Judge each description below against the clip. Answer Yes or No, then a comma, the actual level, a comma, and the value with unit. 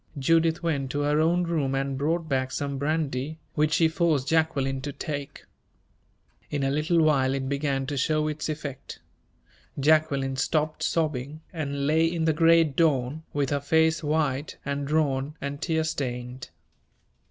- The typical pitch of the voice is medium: Yes, medium, 145 Hz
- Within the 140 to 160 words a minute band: Yes, average, 155 wpm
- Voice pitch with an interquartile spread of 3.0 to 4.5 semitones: No, narrow, 2.6 semitones